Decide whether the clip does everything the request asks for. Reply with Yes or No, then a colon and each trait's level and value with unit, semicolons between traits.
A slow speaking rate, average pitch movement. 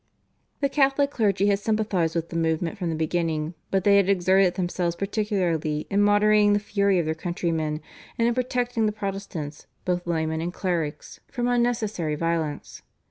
No: average, 165 wpm; average, 4.2 semitones